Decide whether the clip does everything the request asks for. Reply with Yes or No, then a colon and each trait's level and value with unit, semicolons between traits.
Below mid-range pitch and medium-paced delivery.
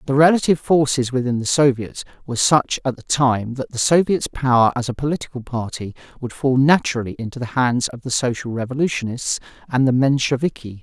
Yes: low, 130 Hz; average, 175 wpm